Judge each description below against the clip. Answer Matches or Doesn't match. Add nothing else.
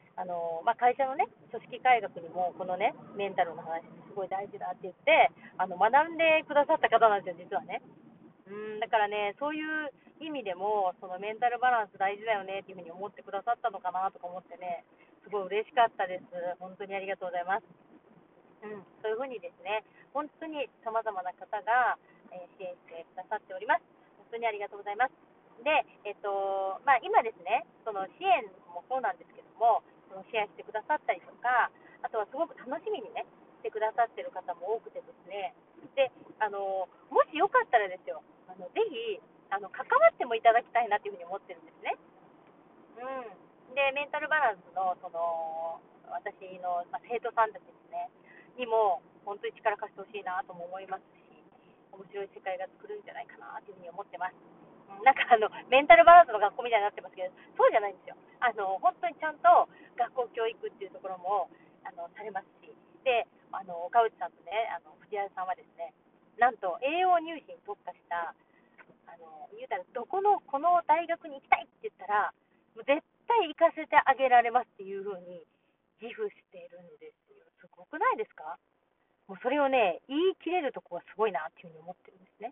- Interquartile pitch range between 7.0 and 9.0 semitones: Matches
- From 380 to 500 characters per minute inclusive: Matches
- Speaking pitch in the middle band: Doesn't match